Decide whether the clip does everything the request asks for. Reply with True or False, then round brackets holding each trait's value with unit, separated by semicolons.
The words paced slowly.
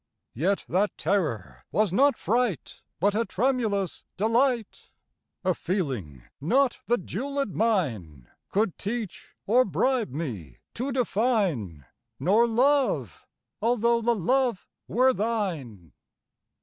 True (105 wpm)